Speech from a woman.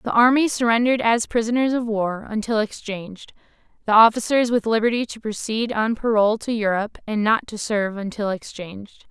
Yes: female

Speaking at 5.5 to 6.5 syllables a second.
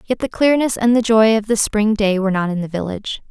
Yes: 6.0 syllables/s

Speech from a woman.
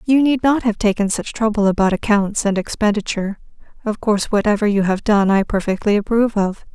Yes: female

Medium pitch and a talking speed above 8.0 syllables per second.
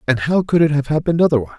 Yes: medium, 145 Hz; 8.3 syllables/s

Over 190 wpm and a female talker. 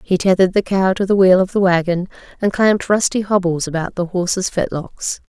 Yes: fast, 205 wpm; female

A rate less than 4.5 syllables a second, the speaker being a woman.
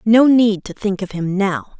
Yes: 4.2 syllables/s; female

